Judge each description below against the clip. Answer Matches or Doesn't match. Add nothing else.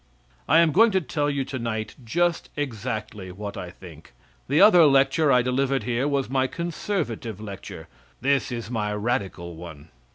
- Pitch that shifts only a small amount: Doesn't match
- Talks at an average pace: Matches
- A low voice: Matches